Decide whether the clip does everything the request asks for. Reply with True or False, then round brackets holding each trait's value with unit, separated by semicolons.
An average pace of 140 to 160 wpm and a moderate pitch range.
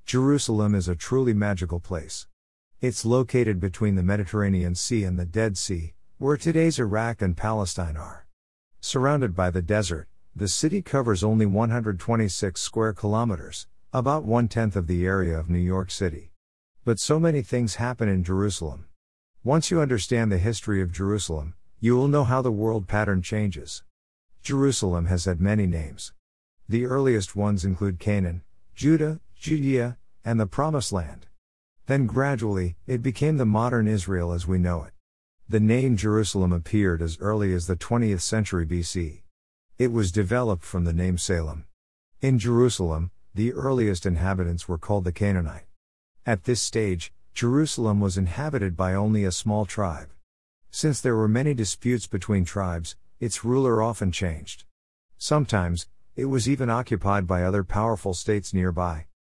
True (155 wpm; 4.9 semitones)